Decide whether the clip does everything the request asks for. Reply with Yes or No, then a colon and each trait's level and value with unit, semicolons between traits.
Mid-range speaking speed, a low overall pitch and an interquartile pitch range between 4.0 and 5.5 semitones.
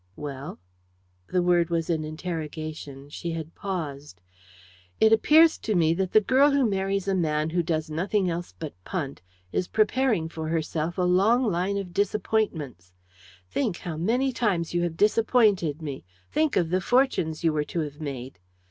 No: average, 165 wpm; medium, 175 Hz; average, 4.6 semitones